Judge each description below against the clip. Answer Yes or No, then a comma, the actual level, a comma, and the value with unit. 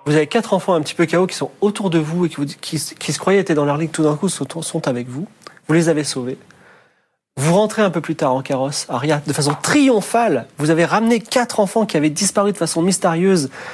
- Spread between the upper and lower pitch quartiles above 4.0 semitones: Yes, average, 4.5 semitones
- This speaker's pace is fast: Yes, fast, 250 wpm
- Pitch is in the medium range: Yes, medium, 165 Hz